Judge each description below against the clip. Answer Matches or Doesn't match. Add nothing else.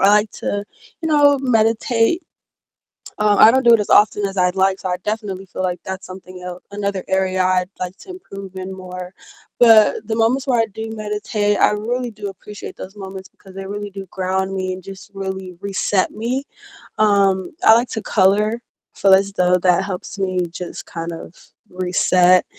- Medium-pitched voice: Doesn't match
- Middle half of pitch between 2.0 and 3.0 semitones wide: Matches